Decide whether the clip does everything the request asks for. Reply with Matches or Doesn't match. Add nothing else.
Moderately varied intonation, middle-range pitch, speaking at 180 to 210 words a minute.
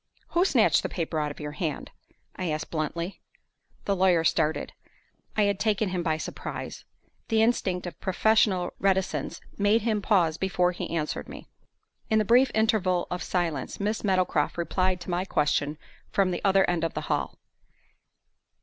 Doesn't match